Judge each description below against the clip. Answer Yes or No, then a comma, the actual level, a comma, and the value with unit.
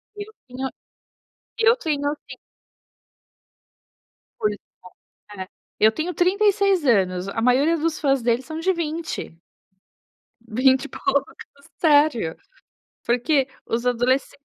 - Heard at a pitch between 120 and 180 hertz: No, very high, 275 Hz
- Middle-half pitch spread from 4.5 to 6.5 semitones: Yes, wide, 5.5 semitones